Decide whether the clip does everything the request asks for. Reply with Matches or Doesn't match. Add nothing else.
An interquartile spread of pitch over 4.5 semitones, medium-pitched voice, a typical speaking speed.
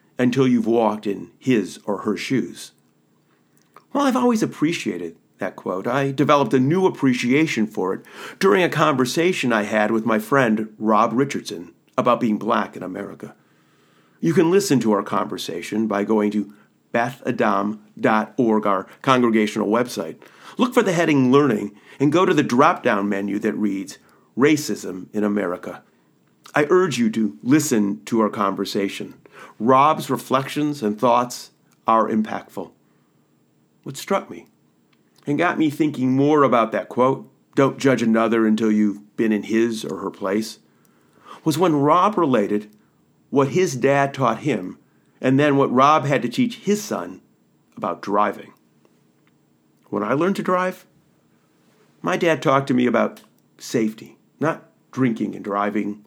Doesn't match